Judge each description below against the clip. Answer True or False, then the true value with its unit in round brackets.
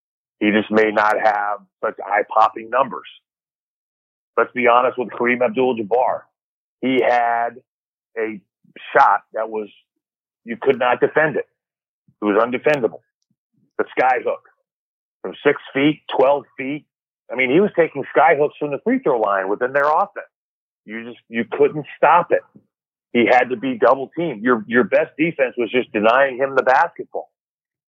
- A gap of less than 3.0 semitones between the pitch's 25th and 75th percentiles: False (4.3 semitones)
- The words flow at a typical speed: True (150 wpm)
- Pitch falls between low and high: False (125 Hz)